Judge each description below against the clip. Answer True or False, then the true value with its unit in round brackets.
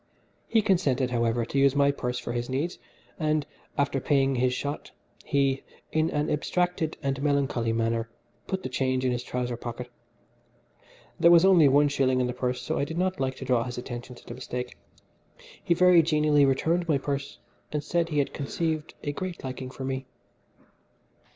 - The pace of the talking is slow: False (185 wpm)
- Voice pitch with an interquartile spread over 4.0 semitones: False (3.5 semitones)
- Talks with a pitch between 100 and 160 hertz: True (140 Hz)